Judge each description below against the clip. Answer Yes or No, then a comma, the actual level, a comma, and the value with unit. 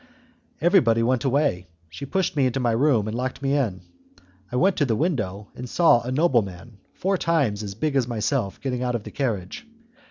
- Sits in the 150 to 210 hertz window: No, low, 125 Hz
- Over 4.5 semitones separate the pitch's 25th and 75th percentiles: Yes, average, 4.9 semitones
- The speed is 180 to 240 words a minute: Yes, average, 195 wpm